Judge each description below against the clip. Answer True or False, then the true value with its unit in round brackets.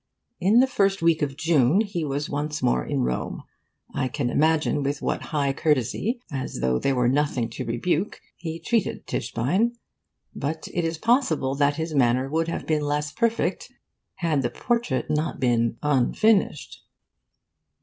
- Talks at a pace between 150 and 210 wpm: True (160 wpm)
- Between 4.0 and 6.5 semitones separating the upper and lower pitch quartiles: True (4.4 semitones)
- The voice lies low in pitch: False (150 Hz)